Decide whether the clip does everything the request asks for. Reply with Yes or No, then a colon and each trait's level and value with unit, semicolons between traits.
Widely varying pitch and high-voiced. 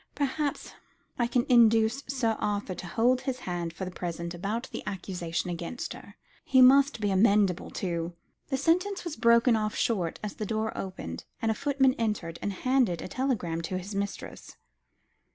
Yes: wide, 6.0 semitones; high, 215 Hz